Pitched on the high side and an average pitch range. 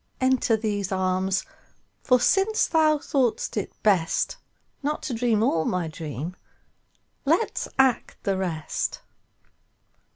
No: high, 215 Hz; wide, 6.3 semitones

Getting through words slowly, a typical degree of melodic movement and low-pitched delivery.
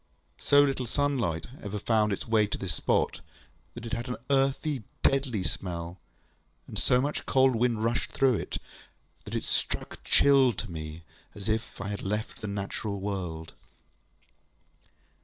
No: average, 155 wpm; average, 4.8 semitones; low, 110 Hz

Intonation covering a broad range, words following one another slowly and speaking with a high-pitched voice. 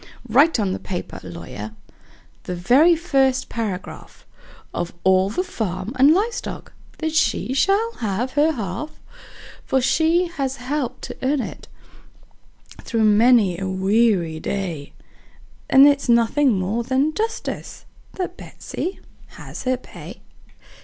Yes: wide, 7.3 semitones; slow, 130 wpm; very high, 250 Hz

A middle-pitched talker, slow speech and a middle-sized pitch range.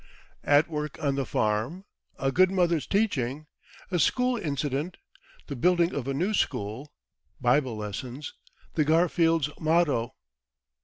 Yes: medium, 150 Hz; slow, 125 wpm; average, 4.6 semitones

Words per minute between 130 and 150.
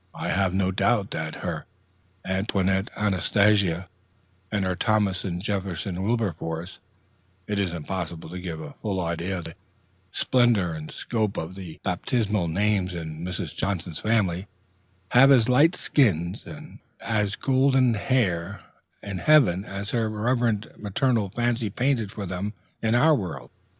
Yes: average, 140 wpm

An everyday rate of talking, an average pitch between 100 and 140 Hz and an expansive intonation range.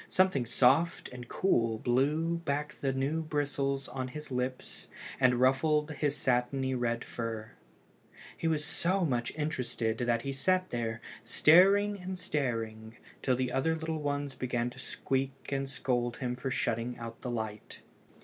No: average, 150 wpm; low, 135 Hz; average, 3.8 semitones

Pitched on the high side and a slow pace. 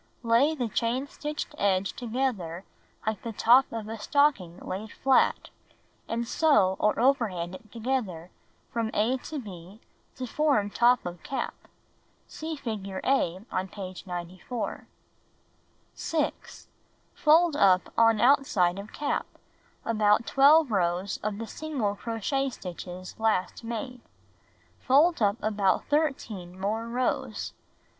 Yes: high, 225 Hz; slow, 125 wpm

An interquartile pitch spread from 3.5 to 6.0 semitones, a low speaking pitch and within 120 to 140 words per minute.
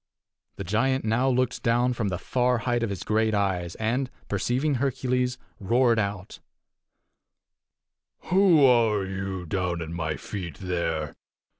Yes: average, 5.1 semitones; low, 110 Hz; slow, 135 wpm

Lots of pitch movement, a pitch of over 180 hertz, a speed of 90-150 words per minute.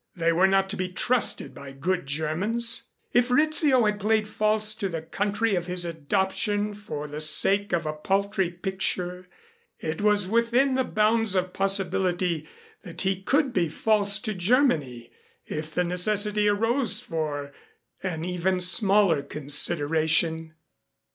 No: average, 4.3 semitones; high, 190 Hz; average, 140 wpm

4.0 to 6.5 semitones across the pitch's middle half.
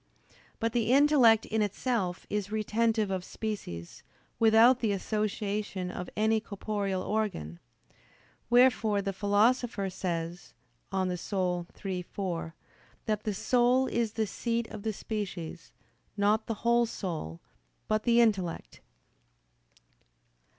No: average, 3.3 semitones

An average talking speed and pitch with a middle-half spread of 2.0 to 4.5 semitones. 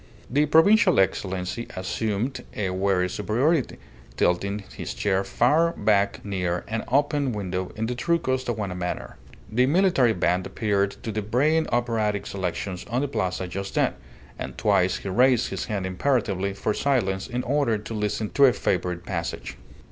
No: average, 155 wpm; average, 5.1 semitones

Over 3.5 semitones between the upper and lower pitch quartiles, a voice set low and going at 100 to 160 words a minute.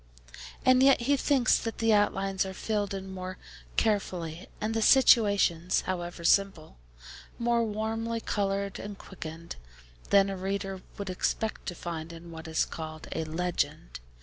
No: average, 4.0 semitones; high, 195 Hz; average, 150 wpm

